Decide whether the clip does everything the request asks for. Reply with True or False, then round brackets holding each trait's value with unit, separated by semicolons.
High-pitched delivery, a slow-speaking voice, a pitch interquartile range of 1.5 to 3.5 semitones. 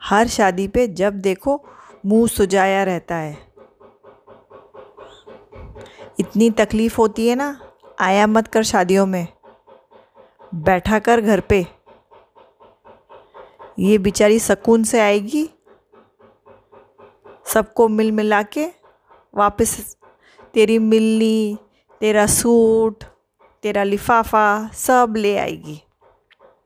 True (220 Hz; 95 wpm; 2.5 semitones)